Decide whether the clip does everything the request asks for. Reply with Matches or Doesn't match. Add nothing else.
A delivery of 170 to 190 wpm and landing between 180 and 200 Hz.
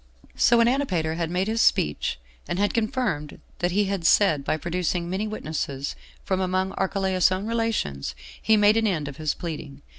Matches